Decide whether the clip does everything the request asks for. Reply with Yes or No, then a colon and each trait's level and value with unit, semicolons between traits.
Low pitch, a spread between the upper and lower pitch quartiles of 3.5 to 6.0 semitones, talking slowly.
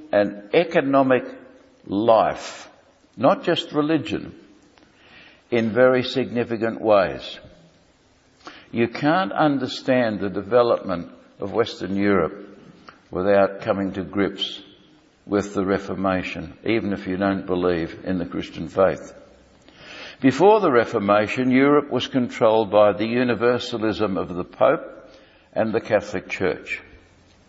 Yes: low, 110 Hz; average, 4.6 semitones; slow, 110 wpm